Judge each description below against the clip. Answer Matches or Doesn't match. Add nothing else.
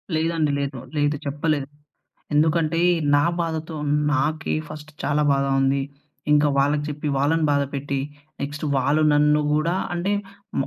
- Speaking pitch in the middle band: Matches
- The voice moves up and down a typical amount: Doesn't match